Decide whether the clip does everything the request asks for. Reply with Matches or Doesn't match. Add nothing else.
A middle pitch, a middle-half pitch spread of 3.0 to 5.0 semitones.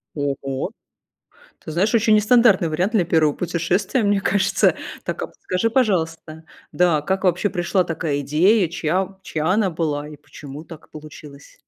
Matches